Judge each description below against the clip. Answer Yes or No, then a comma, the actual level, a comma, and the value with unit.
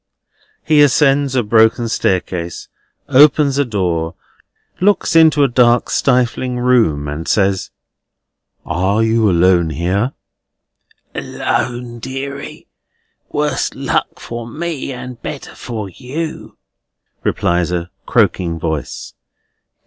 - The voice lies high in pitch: No, low, 120 Hz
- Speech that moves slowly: Yes, slow, 105 wpm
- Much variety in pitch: Yes, wide, 6.7 semitones